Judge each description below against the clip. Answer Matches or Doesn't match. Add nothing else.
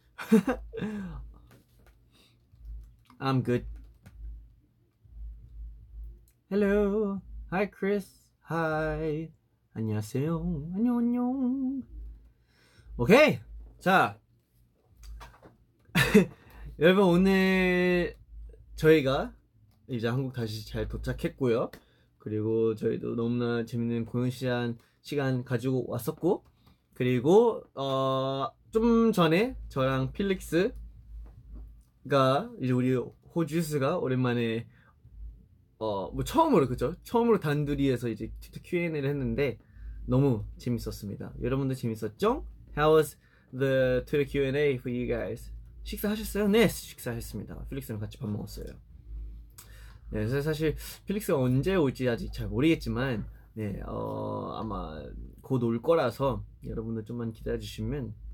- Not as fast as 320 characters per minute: Matches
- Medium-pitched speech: Doesn't match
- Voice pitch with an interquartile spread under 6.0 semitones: Doesn't match